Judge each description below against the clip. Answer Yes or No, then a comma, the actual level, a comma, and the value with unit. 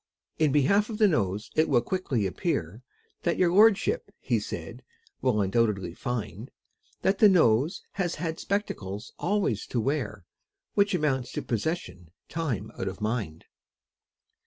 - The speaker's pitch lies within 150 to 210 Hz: No, low, 130 Hz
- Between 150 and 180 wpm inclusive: No, average, 140 wpm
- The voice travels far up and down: Yes, wide, 9.0 semitones